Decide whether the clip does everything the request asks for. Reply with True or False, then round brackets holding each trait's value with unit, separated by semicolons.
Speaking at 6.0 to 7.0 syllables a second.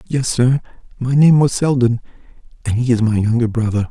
False (5.5 syllables/s)